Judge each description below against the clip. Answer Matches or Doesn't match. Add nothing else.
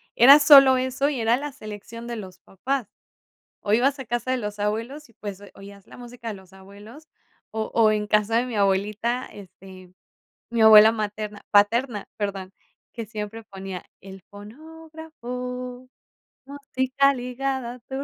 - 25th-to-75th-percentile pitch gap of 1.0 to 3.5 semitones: Doesn't match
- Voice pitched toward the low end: Doesn't match